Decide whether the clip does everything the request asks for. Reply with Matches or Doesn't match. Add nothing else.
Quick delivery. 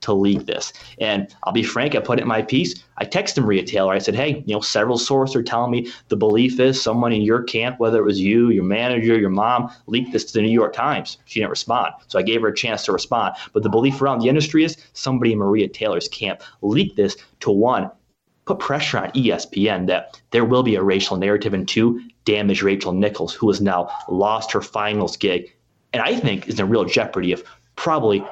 Matches